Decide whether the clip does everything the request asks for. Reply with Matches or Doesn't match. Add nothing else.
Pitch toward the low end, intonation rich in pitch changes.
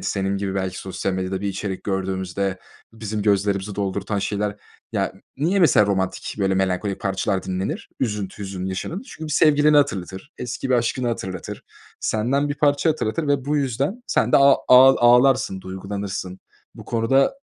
Matches